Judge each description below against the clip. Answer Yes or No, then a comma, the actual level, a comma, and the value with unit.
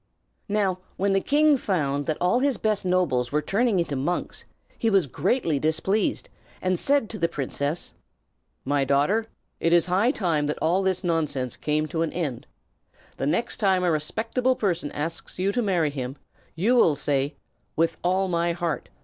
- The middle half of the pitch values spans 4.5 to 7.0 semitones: Yes, average, 5.0 semitones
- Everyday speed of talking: Yes, average, 175 wpm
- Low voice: No, medium, 175 Hz